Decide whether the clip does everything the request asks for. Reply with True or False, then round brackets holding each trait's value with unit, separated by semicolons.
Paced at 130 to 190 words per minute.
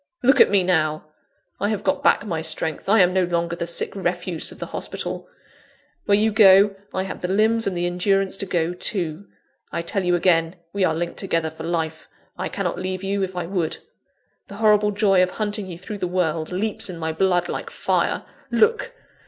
False (205 wpm)